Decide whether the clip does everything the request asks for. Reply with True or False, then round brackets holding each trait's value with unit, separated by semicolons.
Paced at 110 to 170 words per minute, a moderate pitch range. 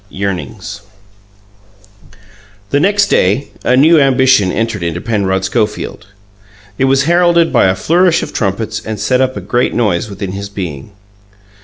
False (145 wpm; 5.7 semitones)